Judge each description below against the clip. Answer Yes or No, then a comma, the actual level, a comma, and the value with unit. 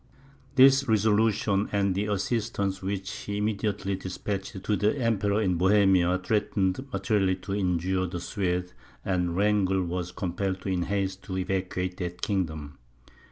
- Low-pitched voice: Yes, very low, 95 Hz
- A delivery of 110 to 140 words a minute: Yes, slow, 135 wpm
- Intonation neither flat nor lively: No, narrow, 2.0 semitones